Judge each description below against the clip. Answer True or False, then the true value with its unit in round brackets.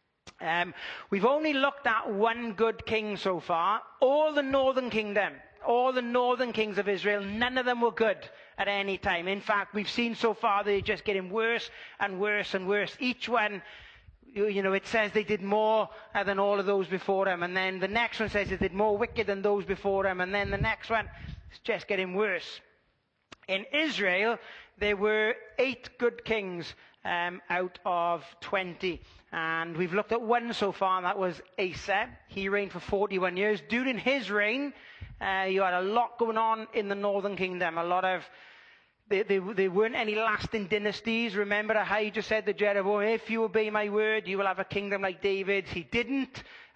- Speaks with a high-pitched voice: True (205 Hz)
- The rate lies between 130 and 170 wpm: False (195 wpm)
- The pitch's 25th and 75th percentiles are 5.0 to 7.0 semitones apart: False (2.8 semitones)